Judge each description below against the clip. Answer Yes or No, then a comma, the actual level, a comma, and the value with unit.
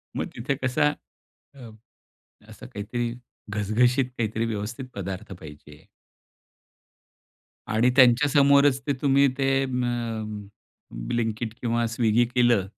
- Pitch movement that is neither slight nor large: Yes, average, 3.4 semitones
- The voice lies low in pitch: Yes, low, 120 Hz